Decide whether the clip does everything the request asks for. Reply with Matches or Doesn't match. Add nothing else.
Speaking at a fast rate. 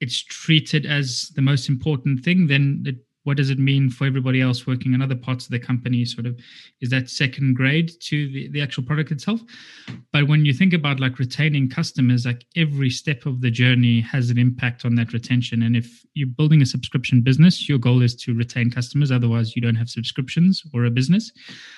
Matches